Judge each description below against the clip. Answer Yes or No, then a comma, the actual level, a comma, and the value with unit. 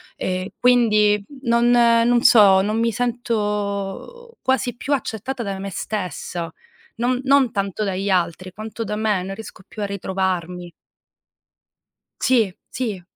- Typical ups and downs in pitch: Yes, average, 3.7 semitones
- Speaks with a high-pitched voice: Yes, high, 210 Hz